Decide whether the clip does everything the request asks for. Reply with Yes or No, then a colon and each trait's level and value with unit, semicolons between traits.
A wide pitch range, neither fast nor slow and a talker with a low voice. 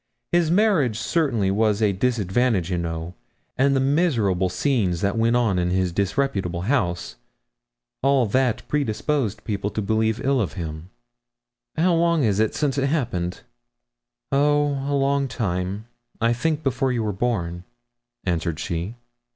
Yes: wide, 6.7 semitones; average, 145 wpm; low, 115 Hz